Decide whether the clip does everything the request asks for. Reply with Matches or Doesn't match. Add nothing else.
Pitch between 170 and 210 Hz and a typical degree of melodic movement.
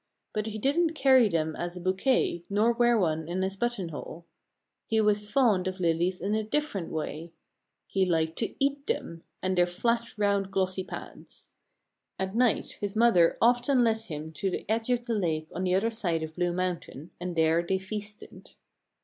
Matches